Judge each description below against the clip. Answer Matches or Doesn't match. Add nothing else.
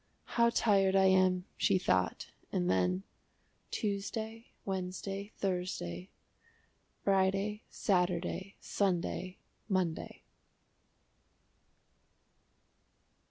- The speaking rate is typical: Doesn't match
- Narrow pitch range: Matches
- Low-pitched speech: Doesn't match